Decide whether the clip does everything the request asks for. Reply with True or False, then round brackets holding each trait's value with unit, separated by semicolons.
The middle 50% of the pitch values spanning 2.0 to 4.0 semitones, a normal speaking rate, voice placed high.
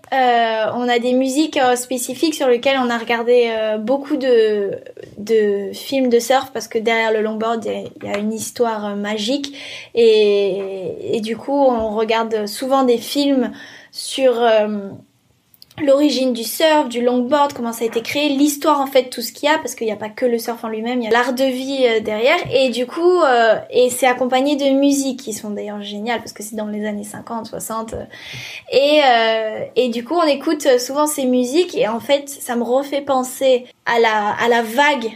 True (3.5 semitones; 205 wpm; 245 Hz)